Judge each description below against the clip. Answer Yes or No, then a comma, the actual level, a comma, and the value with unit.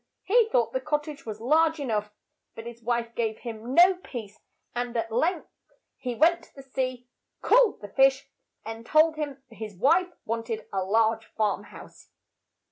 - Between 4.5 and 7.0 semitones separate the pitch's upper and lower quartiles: Yes, average, 5.2 semitones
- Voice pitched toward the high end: Yes, high, 245 Hz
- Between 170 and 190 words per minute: Yes, average, 180 wpm